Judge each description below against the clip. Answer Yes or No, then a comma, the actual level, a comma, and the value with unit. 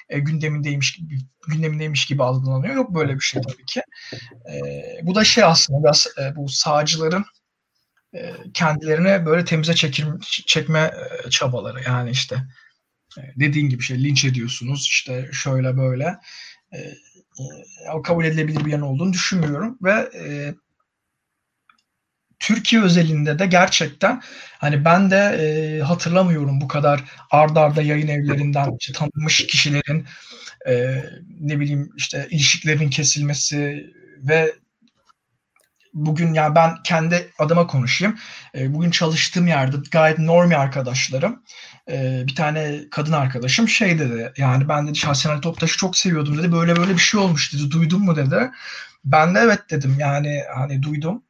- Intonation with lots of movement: No, average, 3.2 semitones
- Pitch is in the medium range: Yes, medium, 150 Hz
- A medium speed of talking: No, fast, 145 wpm